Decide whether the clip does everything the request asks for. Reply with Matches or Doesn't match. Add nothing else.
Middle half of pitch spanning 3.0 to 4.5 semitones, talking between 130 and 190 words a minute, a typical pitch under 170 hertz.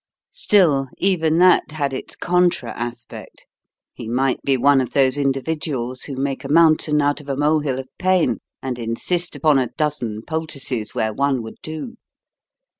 Matches